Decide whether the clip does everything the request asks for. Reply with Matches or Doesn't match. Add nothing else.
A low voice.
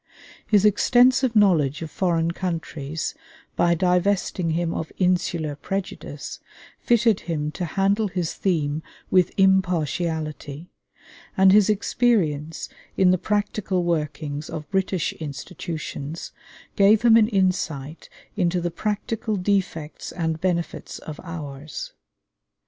Doesn't match